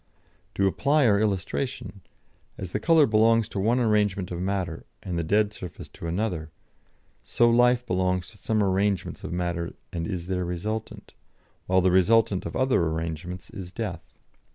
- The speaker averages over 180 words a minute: No, average, 160 wpm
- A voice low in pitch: Yes, very low, 95 Hz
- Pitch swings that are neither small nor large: Yes, average, 3.7 semitones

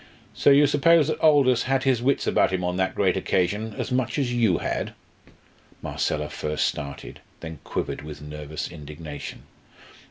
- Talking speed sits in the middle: Yes, average, 160 wpm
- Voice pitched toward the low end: Yes, very low, 95 Hz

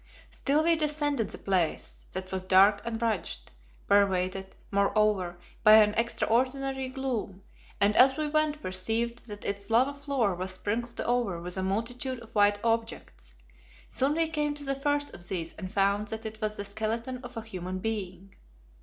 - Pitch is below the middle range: No, high, 220 Hz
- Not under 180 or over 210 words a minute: No, average, 170 wpm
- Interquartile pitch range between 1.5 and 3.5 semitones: No, average, 5.0 semitones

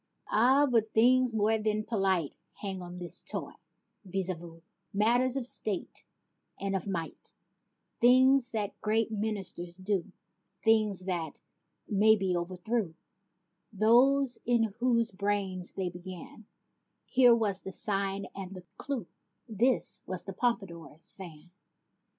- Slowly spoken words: Yes, slow, 125 wpm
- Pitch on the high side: Yes, high, 205 Hz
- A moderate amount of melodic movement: Yes, average, 3.9 semitones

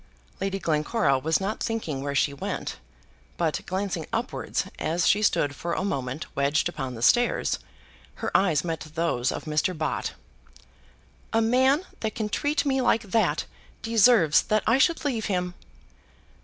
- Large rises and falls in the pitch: Yes, wide, 6.8 semitones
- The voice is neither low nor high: Yes, medium, 180 Hz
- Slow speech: No, average, 155 wpm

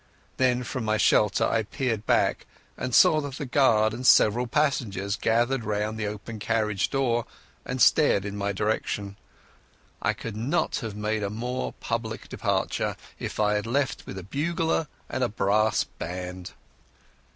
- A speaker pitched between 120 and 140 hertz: No, low, 110 Hz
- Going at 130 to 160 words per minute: Yes, average, 155 wpm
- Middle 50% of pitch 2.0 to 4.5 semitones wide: Yes, average, 3.5 semitones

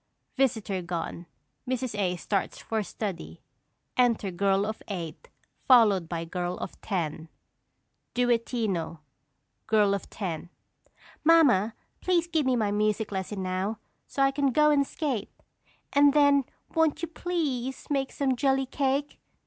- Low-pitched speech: No, high, 225 Hz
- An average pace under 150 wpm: Yes, slow, 135 wpm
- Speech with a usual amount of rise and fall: No, wide, 6.2 semitones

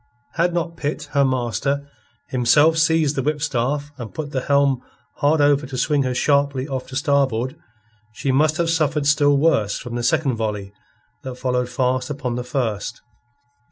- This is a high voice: No, medium, 140 Hz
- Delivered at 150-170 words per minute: Yes, average, 165 wpm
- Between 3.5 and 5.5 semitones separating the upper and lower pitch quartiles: No, average, 2.9 semitones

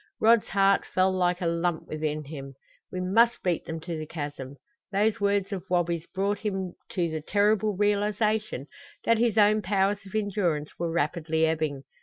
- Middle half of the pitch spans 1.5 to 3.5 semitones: No, average, 4.2 semitones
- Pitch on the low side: No, medium, 185 Hz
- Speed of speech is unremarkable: Yes, average, 170 wpm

